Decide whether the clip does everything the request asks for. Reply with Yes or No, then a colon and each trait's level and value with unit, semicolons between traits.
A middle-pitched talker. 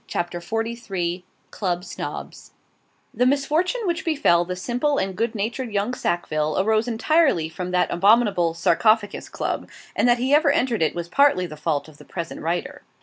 No: high, 210 Hz